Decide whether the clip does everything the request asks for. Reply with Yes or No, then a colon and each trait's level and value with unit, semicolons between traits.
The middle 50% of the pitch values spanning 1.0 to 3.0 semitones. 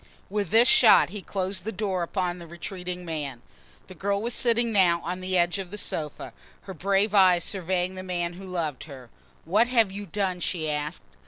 Yes: narrow, 2.6 semitones